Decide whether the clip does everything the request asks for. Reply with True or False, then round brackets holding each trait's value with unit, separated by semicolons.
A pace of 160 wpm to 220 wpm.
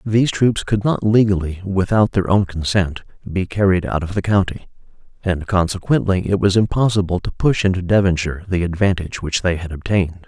True (175 wpm)